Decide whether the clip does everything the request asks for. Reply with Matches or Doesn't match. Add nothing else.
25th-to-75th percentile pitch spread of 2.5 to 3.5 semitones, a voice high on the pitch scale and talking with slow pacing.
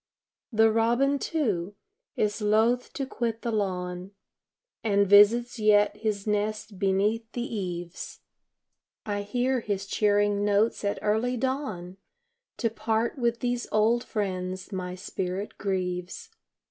Matches